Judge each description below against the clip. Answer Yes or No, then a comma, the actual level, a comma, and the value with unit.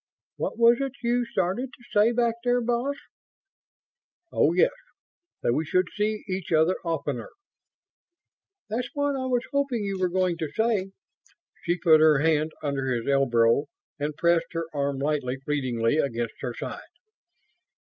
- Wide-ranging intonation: Yes, wide, 8.3 semitones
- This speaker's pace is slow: No, average, 150 wpm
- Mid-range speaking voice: Yes, medium, 175 Hz